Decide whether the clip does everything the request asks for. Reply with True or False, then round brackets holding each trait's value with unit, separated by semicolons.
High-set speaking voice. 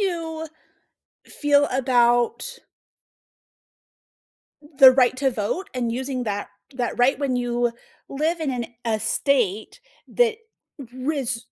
True (260 Hz)